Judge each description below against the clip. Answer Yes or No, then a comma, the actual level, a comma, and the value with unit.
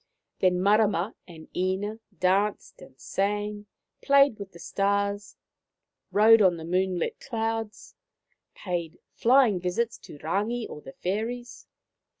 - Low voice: No, high, 200 Hz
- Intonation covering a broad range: No, average, 3.4 semitones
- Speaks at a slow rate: Yes, slow, 120 wpm